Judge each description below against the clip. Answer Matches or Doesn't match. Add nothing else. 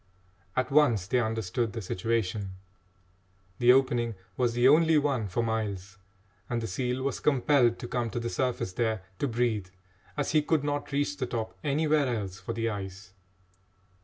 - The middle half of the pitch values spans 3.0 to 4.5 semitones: Matches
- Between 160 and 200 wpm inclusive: Matches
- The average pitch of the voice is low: Matches